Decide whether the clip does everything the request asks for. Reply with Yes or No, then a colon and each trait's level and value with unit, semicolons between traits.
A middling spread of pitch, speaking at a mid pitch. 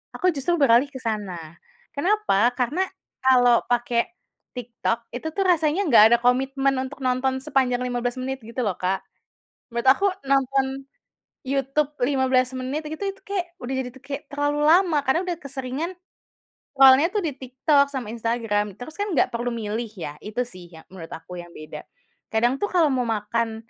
No: average, 3.6 semitones; very high, 260 Hz